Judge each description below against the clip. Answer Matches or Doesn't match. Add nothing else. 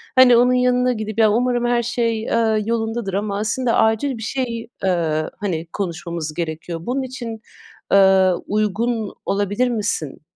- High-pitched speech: Matches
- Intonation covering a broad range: Doesn't match